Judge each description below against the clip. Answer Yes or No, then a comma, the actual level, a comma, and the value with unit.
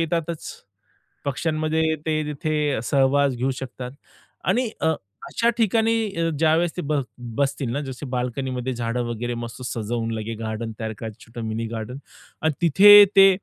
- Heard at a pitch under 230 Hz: Yes, low, 135 Hz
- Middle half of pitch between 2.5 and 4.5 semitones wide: No, average, 5.2 semitones